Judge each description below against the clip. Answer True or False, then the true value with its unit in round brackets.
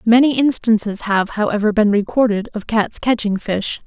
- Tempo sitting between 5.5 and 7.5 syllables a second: False (4.9 syllables/s)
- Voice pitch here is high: True (220 Hz)